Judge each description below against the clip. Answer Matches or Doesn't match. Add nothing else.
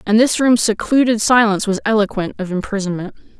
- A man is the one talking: Doesn't match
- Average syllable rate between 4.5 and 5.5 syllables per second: Doesn't match